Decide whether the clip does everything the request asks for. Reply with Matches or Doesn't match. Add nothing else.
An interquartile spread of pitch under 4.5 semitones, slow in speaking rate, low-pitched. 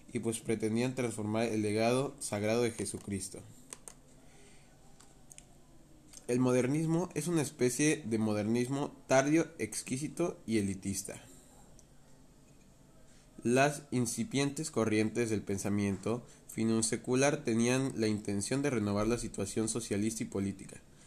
Matches